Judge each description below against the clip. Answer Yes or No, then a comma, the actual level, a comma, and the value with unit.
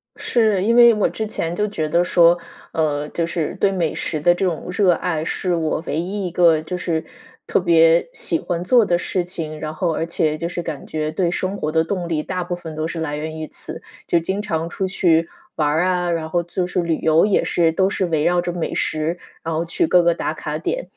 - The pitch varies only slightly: Yes, narrow, 2.3 semitones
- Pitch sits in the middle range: Yes, medium, 170 Hz